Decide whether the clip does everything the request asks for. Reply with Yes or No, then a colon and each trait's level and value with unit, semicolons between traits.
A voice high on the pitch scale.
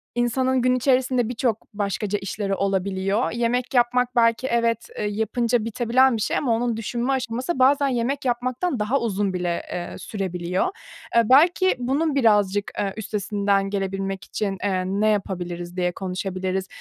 Yes: high, 220 Hz